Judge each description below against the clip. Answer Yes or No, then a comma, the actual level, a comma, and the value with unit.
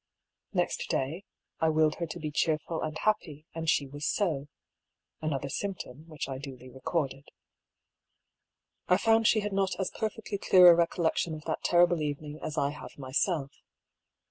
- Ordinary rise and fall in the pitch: Yes, average, 3.5 semitones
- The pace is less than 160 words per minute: No, average, 165 wpm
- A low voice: No, medium, 155 Hz